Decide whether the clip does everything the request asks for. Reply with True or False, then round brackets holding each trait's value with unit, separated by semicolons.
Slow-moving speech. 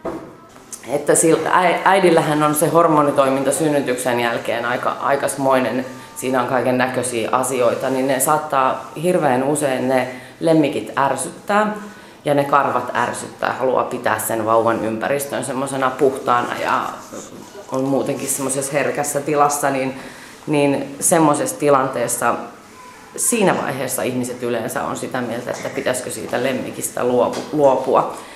False (120 wpm)